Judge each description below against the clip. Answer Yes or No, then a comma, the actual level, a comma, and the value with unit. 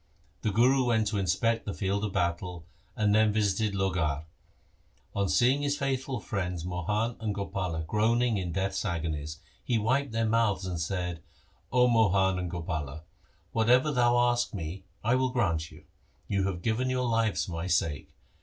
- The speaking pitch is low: Yes, low, 100 Hz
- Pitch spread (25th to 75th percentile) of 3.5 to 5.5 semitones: Yes, average, 4.8 semitones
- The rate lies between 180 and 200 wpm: No, average, 170 wpm